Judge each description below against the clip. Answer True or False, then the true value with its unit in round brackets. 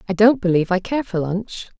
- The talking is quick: True (235 wpm)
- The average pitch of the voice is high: True (200 Hz)